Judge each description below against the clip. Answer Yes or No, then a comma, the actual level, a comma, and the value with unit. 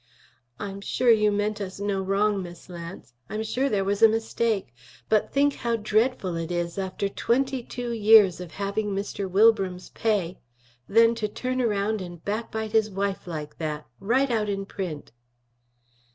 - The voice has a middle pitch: No, high, 205 Hz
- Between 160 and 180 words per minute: Yes, average, 165 wpm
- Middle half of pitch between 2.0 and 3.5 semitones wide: Yes, average, 2.9 semitones